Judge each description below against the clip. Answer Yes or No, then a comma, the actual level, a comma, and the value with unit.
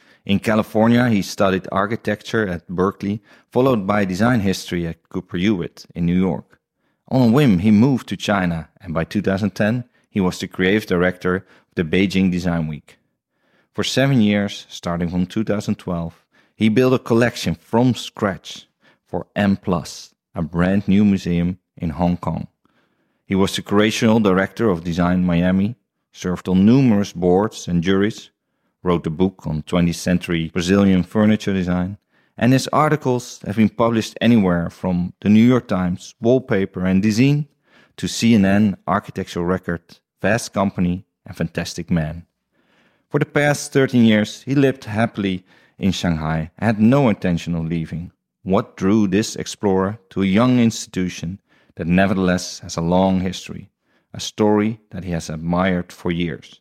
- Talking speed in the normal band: Yes, average, 150 wpm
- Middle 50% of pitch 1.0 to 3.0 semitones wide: No, average, 3.5 semitones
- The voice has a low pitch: Yes, very low, 95 Hz